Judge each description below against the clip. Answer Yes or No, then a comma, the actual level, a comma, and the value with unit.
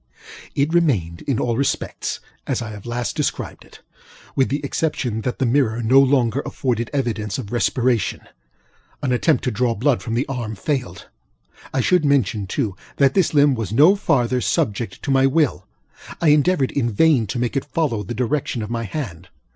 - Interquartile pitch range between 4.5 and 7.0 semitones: No, average, 3.8 semitones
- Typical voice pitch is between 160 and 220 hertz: No, low, 125 Hz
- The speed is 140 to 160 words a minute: No, average, 180 wpm